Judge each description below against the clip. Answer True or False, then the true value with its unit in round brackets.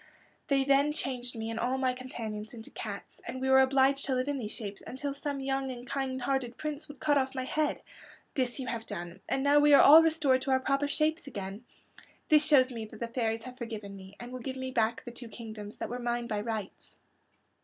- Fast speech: True (230 wpm)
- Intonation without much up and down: False (3.2 semitones)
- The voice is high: True (255 Hz)